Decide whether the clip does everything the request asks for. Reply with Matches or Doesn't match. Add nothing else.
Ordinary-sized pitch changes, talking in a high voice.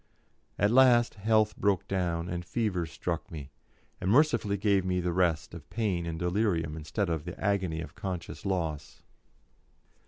Doesn't match